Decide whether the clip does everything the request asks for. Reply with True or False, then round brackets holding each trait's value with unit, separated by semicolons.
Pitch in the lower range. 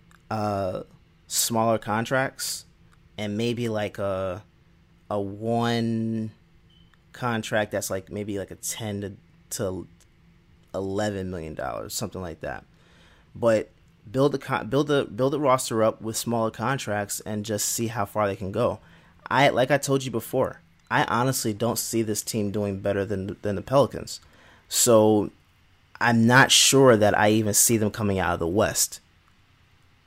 True (105 Hz)